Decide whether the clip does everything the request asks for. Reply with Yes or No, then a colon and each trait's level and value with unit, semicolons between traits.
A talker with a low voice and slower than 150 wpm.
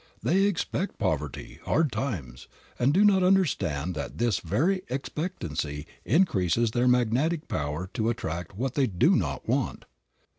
Yes: low, 120 Hz; average, 140 wpm